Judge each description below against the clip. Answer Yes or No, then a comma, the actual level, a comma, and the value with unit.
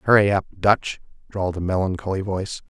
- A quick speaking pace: No, average, 150 wpm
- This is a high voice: No, very low, 95 Hz